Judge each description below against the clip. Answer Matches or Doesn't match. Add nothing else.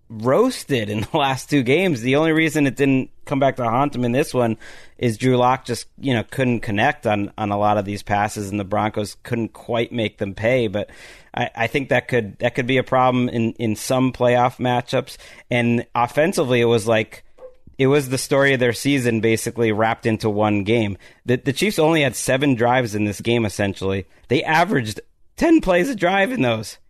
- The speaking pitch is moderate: Doesn't match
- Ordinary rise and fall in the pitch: Matches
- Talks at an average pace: Doesn't match